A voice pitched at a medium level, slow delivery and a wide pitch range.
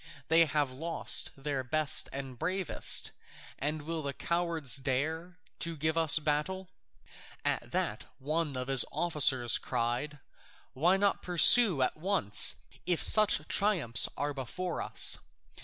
No: medium, 155 Hz; slow, 130 wpm; average, 3.9 semitones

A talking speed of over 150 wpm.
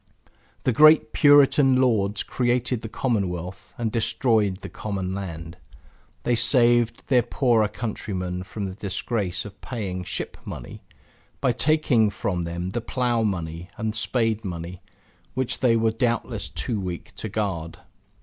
No: average, 140 wpm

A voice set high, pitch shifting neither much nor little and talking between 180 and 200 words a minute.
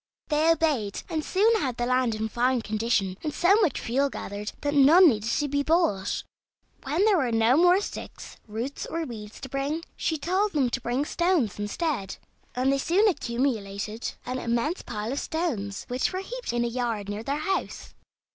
No: very high, 260 Hz; wide, 6.3 semitones; average, 185 wpm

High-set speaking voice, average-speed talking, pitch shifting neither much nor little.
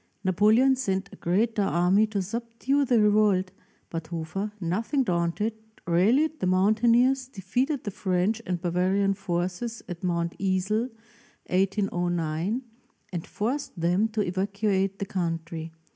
No: high, 195 Hz; slow, 125 wpm; average, 3.9 semitones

